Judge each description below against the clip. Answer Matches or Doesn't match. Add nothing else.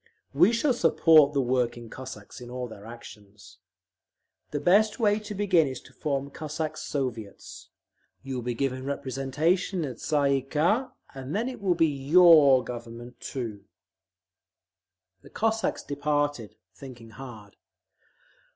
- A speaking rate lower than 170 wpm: Matches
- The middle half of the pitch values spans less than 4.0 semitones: Doesn't match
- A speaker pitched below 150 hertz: Matches